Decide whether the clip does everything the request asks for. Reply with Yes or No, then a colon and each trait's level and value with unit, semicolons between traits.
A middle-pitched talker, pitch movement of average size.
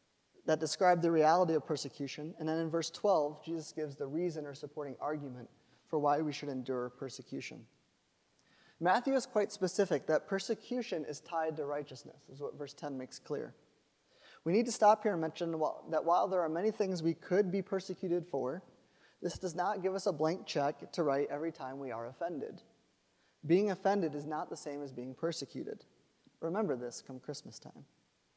Yes: medium, 160 Hz; average, 4.4 semitones